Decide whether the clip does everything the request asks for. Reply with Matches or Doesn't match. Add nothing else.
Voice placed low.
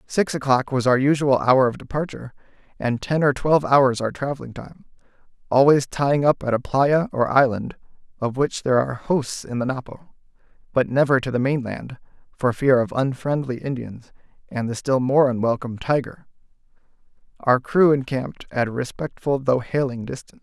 Matches